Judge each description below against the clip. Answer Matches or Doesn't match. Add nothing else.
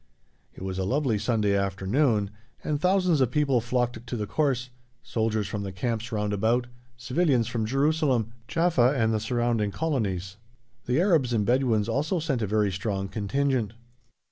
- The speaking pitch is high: Doesn't match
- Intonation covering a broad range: Doesn't match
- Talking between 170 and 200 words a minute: Doesn't match